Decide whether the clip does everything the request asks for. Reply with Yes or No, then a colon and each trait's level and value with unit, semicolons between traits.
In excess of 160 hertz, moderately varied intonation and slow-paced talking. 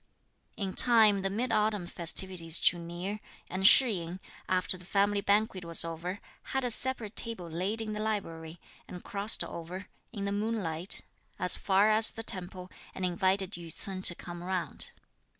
No: high, 190 Hz; average, 3.3 semitones; average, 170 wpm